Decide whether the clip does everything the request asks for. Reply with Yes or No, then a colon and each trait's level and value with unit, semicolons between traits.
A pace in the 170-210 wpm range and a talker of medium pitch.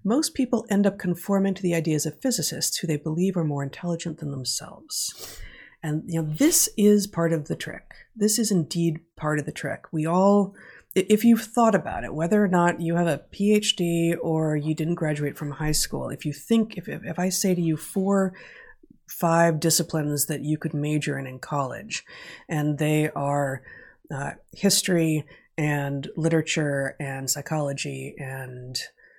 Yes: average, 175 wpm; medium, 165 Hz